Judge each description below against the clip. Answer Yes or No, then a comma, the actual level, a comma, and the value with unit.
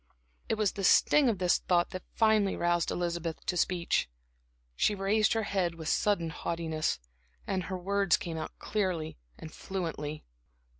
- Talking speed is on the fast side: No, average, 150 wpm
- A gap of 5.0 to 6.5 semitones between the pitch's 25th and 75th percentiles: No, average, 3.1 semitones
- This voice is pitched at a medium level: Yes, medium, 180 Hz